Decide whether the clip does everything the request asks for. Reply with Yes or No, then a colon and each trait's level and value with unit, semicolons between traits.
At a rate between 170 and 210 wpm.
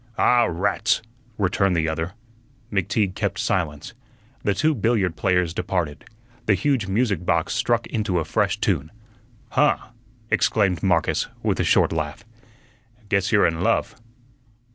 No: slow, 135 wpm